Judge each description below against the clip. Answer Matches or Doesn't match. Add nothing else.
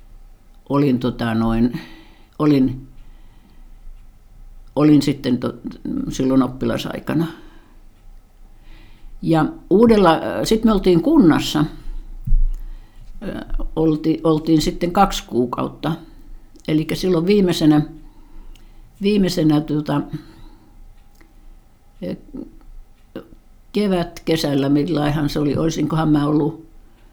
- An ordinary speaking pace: Doesn't match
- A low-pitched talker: Doesn't match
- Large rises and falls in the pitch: Matches